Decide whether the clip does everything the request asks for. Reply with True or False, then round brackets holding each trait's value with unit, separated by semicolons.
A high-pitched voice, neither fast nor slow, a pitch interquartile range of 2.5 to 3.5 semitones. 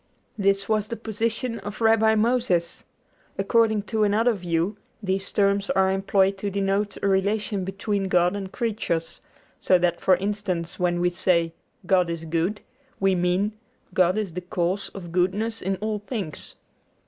True (195 Hz; 155 wpm; 2.8 semitones)